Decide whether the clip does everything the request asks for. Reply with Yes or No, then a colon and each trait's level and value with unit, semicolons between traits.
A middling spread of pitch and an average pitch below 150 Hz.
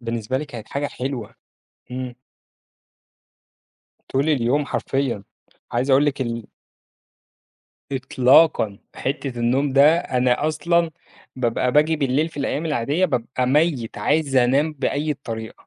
Yes: average, 3.3 semitones; low, 135 Hz